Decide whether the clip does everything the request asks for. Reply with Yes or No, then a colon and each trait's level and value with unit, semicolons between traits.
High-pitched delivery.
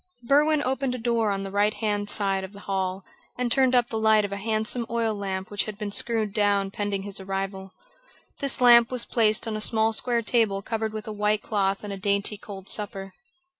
Yes: high, 210 Hz